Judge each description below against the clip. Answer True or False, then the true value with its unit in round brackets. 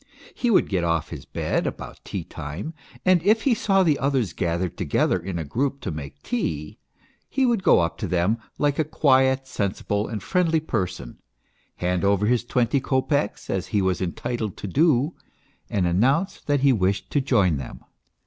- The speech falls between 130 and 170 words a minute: False (180 wpm)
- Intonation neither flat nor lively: False (8.0 semitones)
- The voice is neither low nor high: False (110 Hz)